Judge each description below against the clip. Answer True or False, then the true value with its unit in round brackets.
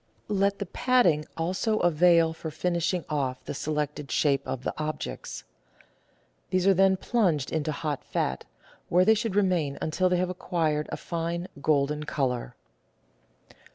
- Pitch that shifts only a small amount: False (3.7 semitones)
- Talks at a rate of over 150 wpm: False (145 wpm)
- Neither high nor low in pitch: True (165 Hz)